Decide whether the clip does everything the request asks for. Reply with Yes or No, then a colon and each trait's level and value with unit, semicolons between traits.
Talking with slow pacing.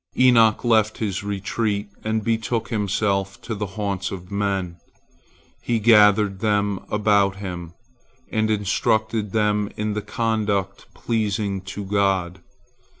Yes: slow, 120 wpm